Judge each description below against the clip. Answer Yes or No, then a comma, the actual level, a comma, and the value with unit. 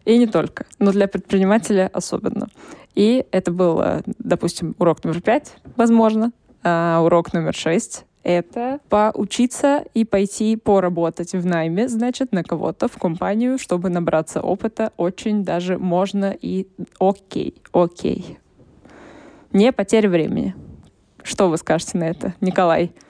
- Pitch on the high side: Yes, high, 195 Hz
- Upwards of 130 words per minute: No, average, 125 wpm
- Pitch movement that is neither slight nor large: Yes, average, 4.5 semitones